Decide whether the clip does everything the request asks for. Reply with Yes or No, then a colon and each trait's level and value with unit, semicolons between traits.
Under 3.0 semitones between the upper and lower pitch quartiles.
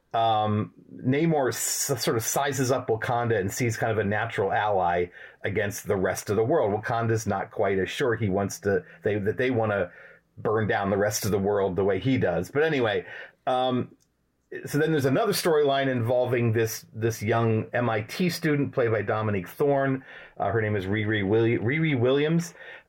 No: average, 4.1 semitones